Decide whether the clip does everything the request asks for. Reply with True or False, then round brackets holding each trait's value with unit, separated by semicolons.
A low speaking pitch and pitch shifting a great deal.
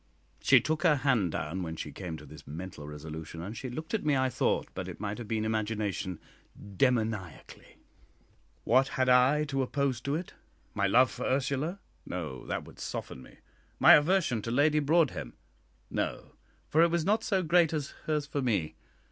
True (125 Hz; 7.5 semitones)